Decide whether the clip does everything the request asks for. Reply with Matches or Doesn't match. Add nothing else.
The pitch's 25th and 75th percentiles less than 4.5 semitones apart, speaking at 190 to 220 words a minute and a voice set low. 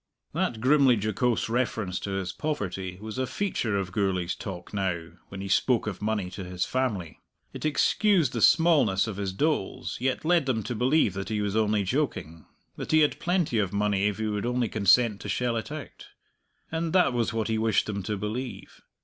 Doesn't match